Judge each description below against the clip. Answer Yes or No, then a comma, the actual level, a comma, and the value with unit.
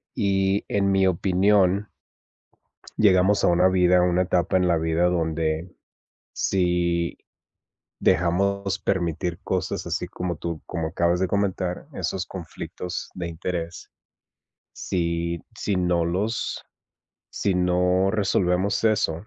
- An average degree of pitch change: No, narrow, 2.2 semitones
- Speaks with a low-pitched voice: Yes, very low, 90 Hz